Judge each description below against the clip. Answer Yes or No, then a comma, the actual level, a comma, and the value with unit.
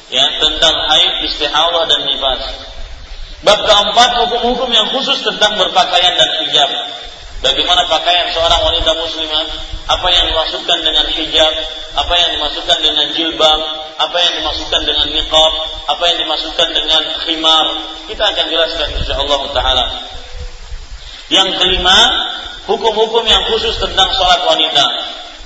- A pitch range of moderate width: Yes, average, 3.5 semitones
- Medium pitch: Yes, medium, 160 Hz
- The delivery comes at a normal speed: Yes, average, 125 wpm